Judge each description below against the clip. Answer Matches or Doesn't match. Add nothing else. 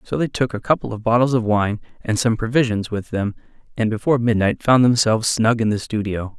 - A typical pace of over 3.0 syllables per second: Matches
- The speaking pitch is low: Matches